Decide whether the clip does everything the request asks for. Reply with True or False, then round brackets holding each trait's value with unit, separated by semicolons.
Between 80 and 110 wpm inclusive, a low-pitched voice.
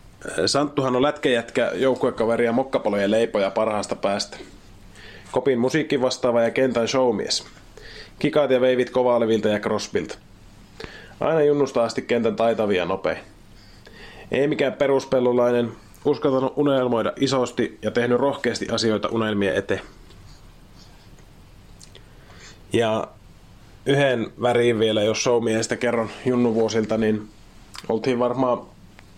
True (105 wpm; 120 Hz)